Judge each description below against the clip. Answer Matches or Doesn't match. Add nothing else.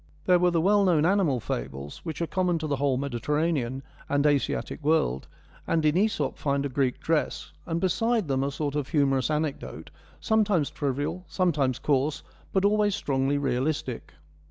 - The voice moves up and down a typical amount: Matches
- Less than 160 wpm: Doesn't match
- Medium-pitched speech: Matches